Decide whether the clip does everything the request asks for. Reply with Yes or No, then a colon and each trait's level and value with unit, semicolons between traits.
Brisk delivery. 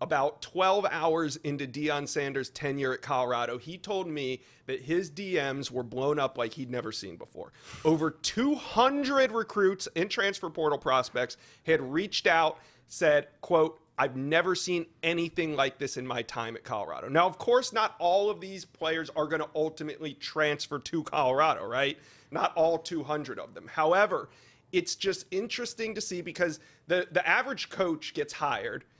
No: average, 165 wpm